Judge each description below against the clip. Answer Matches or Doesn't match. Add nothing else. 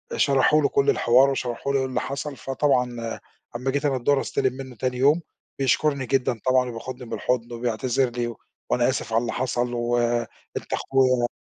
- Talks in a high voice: Doesn't match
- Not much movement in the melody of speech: Matches